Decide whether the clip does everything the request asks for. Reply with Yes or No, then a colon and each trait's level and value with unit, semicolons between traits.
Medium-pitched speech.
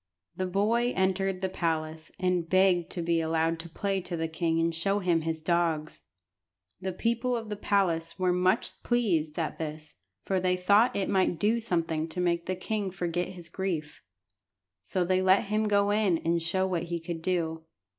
Yes: medium, 180 Hz